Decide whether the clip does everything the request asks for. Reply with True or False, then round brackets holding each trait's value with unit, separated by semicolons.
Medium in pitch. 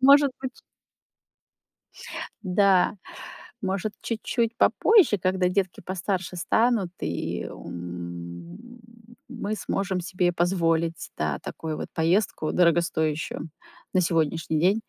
True (180 Hz)